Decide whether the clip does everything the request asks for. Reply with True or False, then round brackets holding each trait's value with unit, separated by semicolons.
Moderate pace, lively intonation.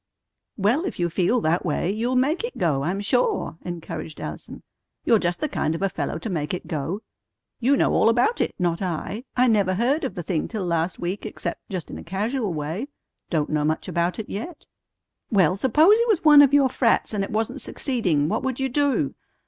False (215 wpm; 7.0 semitones)